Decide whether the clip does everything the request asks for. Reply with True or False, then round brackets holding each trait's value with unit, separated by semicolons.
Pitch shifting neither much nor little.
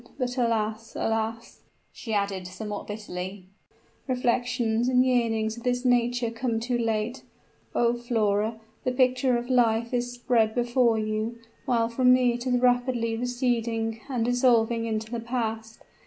False (1.8 semitones)